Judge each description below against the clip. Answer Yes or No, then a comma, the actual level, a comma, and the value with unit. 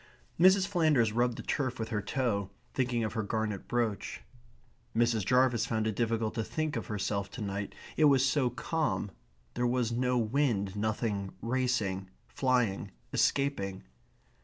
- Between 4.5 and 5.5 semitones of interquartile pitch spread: No, average, 3.5 semitones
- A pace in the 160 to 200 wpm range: No, average, 150 wpm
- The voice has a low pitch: Yes, low, 115 Hz